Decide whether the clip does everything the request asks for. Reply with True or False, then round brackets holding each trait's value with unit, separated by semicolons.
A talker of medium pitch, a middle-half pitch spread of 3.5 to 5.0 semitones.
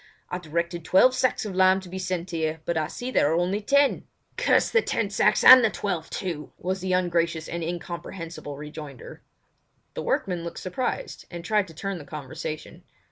False (175 Hz; 2.8 semitones)